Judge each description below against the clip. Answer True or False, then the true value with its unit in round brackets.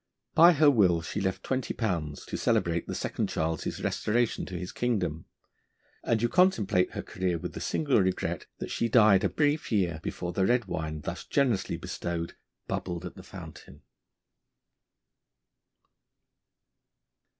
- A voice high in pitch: False (95 Hz)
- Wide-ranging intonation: True (5.8 semitones)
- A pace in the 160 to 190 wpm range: False (145 wpm)